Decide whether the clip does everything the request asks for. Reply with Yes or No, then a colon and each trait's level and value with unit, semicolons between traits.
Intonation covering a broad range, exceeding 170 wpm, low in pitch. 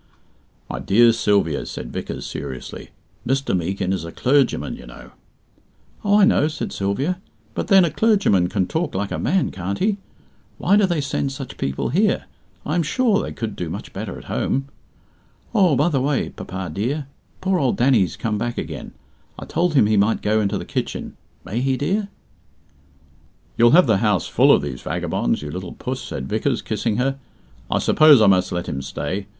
Yes: wide, 8.4 semitones; average, 190 wpm; low, 120 Hz